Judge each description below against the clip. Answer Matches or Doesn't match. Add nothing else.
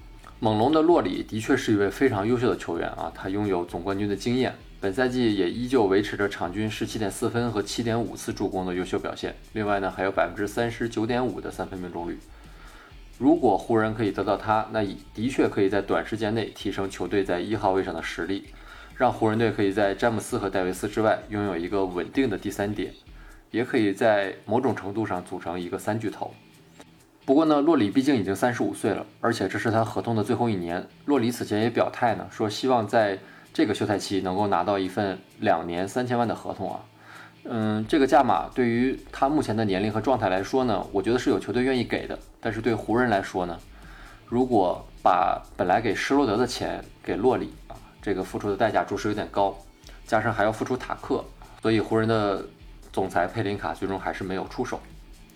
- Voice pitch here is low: Matches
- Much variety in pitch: Doesn't match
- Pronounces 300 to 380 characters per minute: Matches